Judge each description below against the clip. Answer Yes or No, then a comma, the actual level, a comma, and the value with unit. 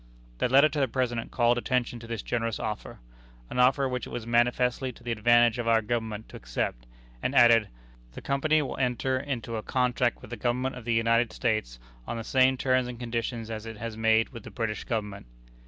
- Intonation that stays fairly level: Yes, narrow, 2.0 semitones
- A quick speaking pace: Yes, fast, 210 wpm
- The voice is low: Yes, low, 120 Hz